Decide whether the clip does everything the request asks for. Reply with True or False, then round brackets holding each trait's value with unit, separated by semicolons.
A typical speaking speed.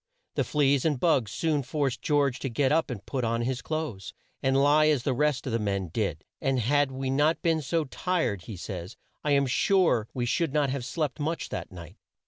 False (215 wpm)